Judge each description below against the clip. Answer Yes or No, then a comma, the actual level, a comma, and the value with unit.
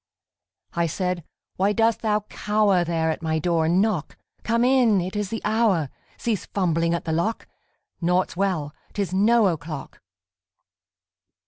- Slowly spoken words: No, average, 145 wpm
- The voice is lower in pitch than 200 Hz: Yes, medium, 185 Hz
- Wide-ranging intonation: No, average, 4.2 semitones